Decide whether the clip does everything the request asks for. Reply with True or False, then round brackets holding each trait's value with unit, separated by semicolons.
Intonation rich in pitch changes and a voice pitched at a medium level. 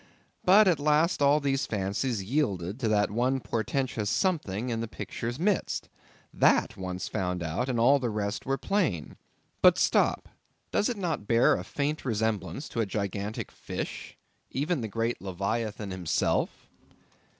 False (6.0 semitones; 115 Hz)